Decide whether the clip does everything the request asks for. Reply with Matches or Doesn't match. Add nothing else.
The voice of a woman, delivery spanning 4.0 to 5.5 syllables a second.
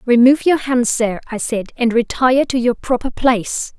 Matches